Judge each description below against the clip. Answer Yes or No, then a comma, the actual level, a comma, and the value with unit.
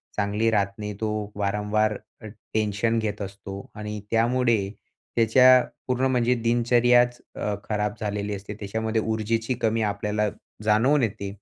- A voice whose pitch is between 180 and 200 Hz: No, low, 110 Hz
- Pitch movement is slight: Yes, narrow, 2.0 semitones